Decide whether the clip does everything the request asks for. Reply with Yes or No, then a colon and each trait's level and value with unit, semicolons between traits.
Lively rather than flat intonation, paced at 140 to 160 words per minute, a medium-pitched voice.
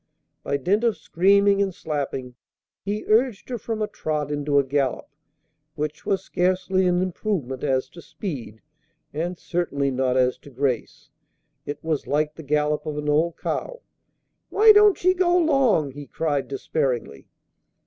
Yes: wide, 6.1 semitones; average, 155 wpm; medium, 155 Hz